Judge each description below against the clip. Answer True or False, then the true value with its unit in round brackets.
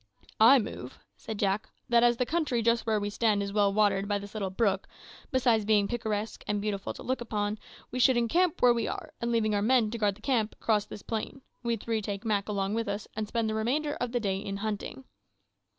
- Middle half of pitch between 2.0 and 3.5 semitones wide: True (2.6 semitones)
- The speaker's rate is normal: False (230 wpm)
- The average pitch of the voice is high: True (220 Hz)